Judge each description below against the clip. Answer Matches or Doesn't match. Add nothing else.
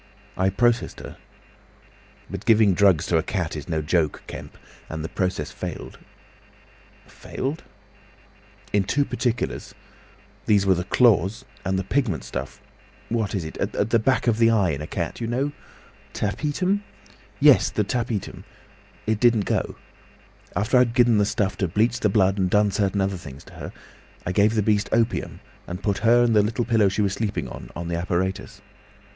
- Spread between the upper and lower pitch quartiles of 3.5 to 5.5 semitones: Matches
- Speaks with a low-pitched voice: Matches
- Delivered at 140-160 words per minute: Doesn't match